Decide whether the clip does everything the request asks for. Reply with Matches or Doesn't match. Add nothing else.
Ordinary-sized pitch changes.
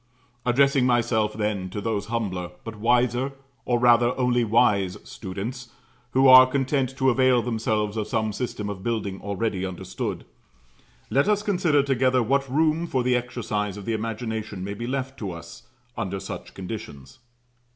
Matches